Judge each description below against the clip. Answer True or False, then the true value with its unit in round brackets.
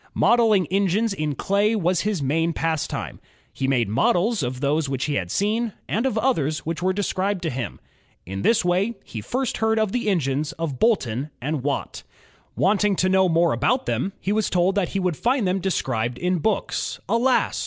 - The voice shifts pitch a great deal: True (6.2 semitones)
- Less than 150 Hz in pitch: False (185 Hz)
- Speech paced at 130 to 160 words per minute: False (190 wpm)